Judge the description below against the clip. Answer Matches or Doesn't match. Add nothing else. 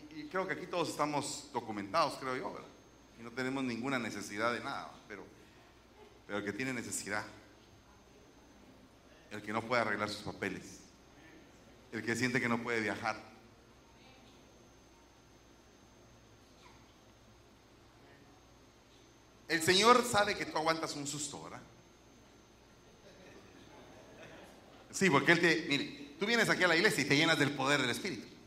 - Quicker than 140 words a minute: Doesn't match